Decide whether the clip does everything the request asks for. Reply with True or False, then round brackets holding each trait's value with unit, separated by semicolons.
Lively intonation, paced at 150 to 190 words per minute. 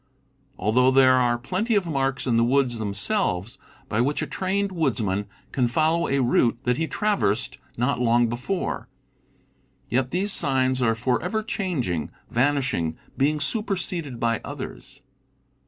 False (5.9 semitones; 140 wpm)